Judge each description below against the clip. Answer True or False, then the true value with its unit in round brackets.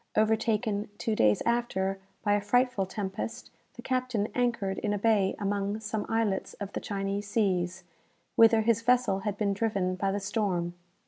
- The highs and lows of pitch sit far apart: False (2.6 semitones)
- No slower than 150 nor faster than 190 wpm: True (165 wpm)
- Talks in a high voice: True (205 Hz)